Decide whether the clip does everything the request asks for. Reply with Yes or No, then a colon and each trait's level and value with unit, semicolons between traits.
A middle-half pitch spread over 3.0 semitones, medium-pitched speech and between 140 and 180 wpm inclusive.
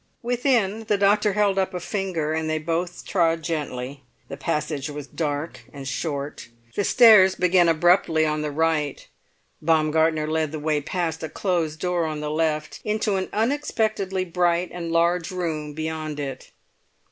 Yes: average, 3.5 semitones; medium, 165 Hz; average, 160 wpm